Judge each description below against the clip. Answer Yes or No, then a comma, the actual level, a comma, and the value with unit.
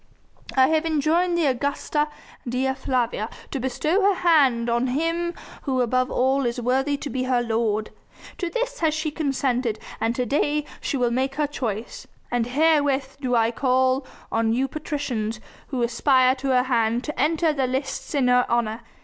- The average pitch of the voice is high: Yes, very high, 260 Hz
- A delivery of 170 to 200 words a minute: Yes, average, 175 wpm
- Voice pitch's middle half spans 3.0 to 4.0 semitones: Yes, average, 3.5 semitones